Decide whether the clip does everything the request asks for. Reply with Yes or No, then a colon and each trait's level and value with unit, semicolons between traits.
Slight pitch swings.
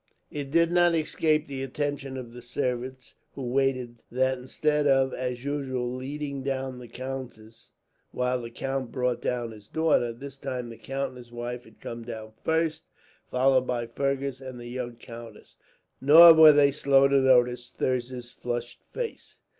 Yes: narrow, 2.2 semitones